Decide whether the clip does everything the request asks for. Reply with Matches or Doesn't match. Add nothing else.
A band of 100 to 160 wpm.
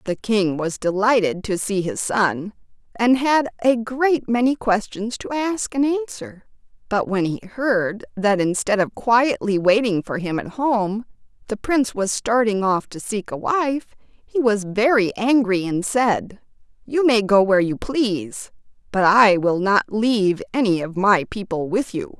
Doesn't match